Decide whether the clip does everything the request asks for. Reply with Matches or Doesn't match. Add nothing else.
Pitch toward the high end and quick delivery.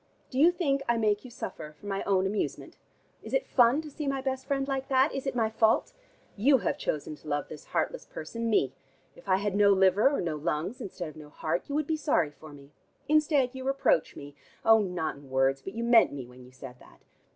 Matches